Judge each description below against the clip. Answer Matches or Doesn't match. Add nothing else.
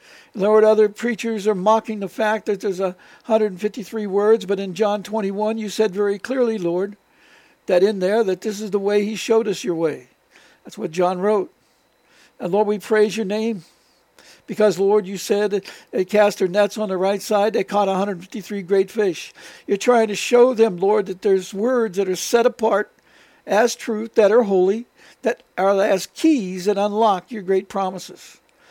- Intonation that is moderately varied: Doesn't match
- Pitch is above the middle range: Matches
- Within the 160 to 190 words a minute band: Matches